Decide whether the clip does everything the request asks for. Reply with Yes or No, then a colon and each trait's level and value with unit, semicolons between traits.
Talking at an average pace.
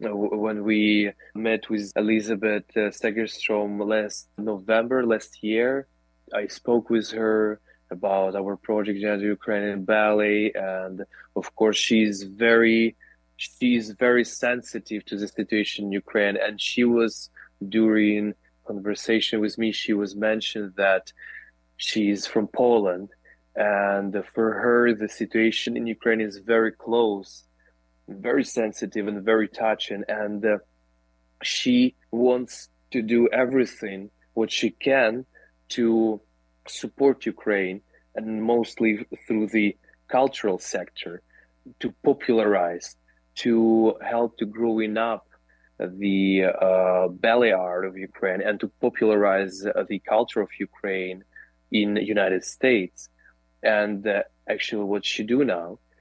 No: slow, 120 wpm